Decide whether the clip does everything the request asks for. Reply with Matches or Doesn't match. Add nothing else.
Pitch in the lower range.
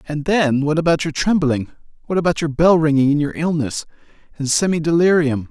Doesn't match